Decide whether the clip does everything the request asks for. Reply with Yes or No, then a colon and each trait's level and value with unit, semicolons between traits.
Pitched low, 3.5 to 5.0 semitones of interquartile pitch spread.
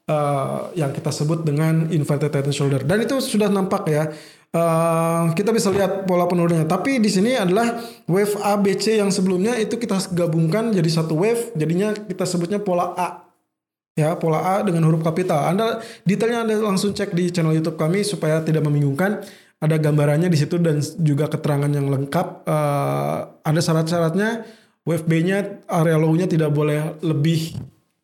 No: medium, 170 Hz; average, 4.2 semitones